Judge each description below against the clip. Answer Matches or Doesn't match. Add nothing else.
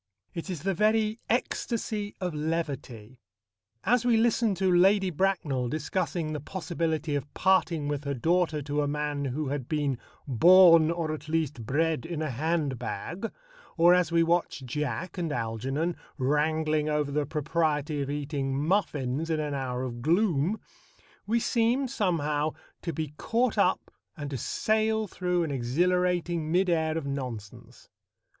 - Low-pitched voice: Doesn't match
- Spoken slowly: Doesn't match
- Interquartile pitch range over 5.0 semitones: Doesn't match